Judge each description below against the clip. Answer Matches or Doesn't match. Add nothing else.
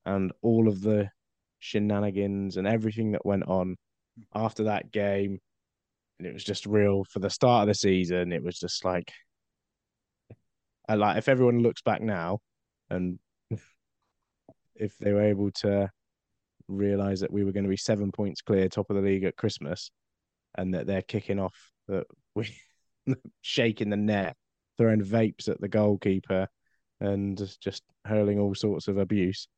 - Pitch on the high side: Doesn't match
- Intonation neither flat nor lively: Doesn't match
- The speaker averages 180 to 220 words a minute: Doesn't match